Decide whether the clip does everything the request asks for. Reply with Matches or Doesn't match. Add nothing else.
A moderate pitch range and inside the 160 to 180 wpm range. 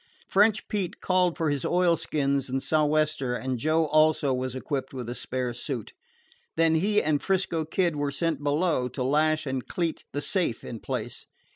Matches